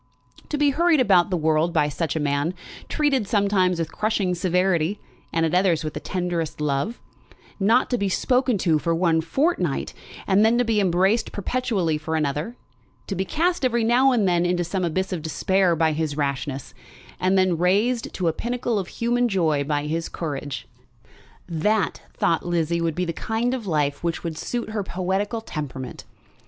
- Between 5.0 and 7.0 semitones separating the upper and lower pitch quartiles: Yes, average, 5.3 semitones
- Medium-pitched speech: Yes, medium, 180 Hz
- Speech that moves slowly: No, average, 180 wpm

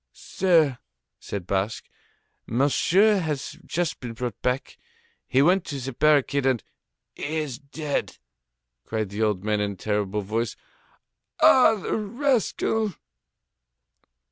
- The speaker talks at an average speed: No, slow, 120 wpm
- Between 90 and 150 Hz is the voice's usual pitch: Yes, low, 135 Hz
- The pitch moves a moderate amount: No, wide, 7.6 semitones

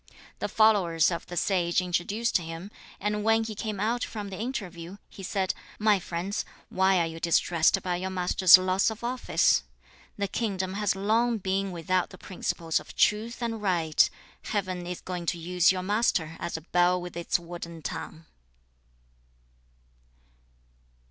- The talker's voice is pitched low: No, medium, 185 Hz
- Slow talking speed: No, average, 155 wpm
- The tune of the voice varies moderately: Yes, average, 3.2 semitones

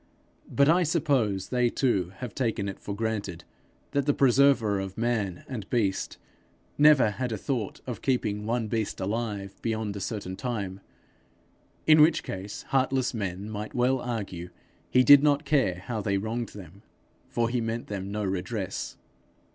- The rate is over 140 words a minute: Yes, average, 160 wpm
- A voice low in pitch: Yes, low, 110 Hz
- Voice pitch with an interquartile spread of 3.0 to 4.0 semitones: No, average, 4.4 semitones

